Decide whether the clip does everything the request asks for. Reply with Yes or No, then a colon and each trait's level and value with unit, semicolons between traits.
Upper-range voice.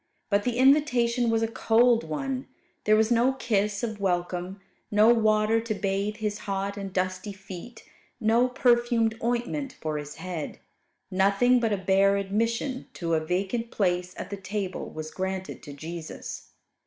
Yes: high, 210 Hz